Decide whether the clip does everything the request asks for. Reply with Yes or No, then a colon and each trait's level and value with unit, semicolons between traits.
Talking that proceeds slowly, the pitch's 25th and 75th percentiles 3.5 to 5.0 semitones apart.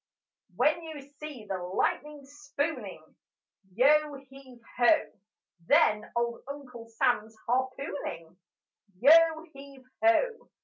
Yes: slow, 95 wpm; average, 4.3 semitones